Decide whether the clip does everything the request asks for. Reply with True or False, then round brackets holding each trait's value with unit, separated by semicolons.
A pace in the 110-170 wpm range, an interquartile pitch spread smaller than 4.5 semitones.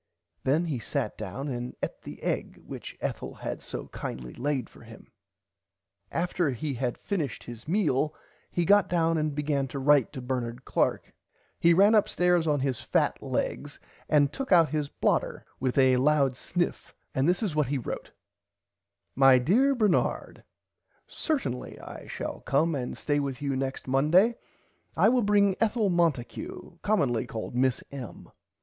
False (160 wpm; 5.0 semitones)